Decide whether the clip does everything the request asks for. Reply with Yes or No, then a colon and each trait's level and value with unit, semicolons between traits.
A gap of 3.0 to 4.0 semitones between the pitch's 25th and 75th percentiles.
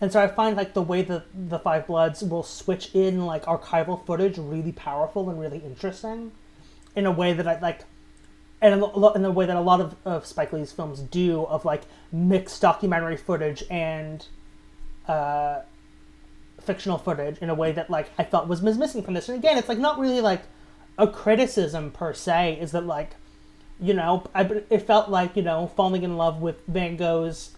Yes: average, 3.5 semitones